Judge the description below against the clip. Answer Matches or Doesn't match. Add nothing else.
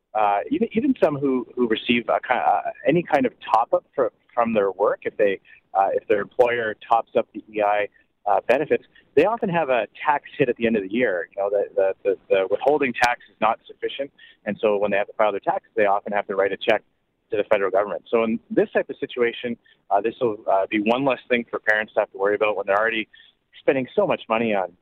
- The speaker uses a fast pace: Matches